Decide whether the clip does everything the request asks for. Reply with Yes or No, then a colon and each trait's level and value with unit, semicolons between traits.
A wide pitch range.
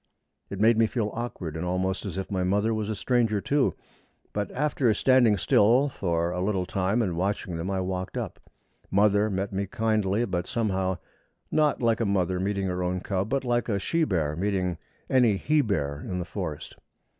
No: average, 3.5 semitones